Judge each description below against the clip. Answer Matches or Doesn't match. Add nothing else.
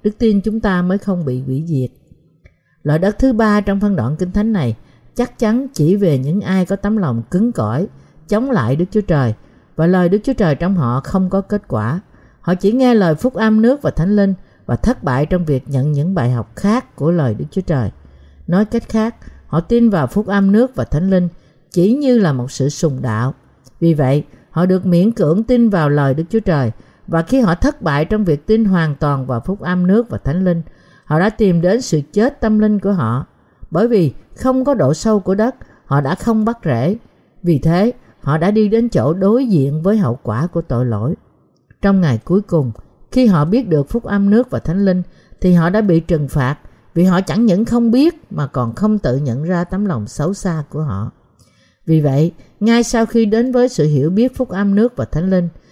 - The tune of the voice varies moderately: Doesn't match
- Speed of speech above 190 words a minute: Matches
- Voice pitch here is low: Doesn't match